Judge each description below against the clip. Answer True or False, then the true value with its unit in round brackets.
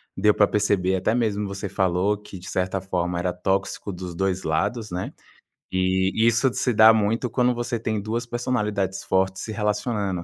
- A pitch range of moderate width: True (3.0 semitones)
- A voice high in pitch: False (100 Hz)